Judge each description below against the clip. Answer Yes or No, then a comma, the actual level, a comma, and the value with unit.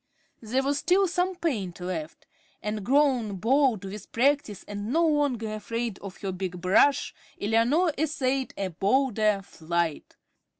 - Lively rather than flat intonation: Yes, wide, 6.2 semitones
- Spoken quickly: No, slow, 135 wpm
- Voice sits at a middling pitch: No, high, 225 Hz